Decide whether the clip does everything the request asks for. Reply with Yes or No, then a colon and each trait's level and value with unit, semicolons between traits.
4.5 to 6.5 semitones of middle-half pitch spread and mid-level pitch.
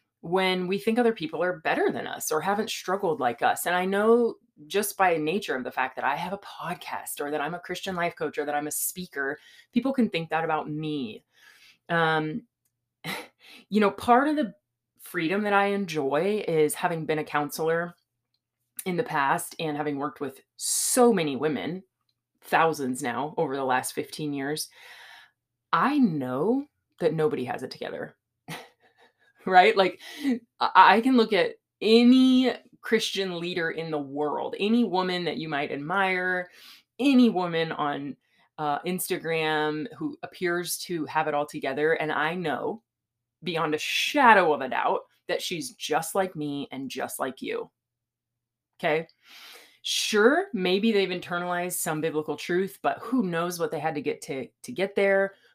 Yes: average, 5.2 semitones; medium, 170 Hz